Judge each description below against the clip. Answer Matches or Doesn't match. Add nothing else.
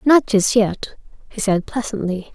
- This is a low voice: Doesn't match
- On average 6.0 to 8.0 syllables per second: Doesn't match